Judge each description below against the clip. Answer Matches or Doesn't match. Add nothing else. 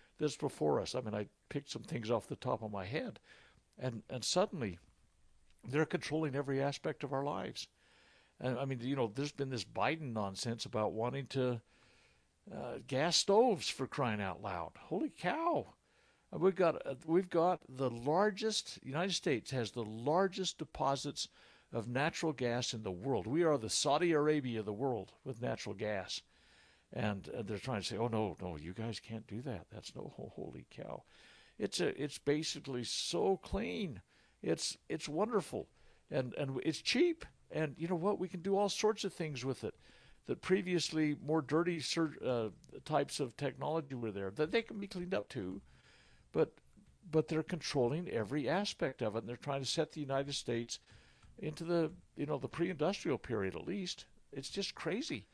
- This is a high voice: Doesn't match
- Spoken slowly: Doesn't match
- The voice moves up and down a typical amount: Doesn't match